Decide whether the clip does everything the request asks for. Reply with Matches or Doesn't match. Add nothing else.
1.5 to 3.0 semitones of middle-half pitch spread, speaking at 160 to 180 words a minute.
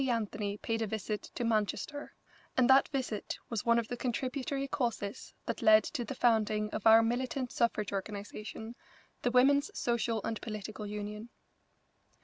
Doesn't match